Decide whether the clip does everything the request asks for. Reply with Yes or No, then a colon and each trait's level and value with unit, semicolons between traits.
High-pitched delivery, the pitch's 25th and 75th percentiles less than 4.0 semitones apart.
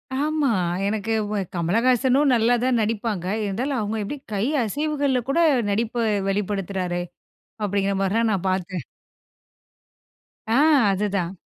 No: high, 215 Hz; average, 4.5 semitones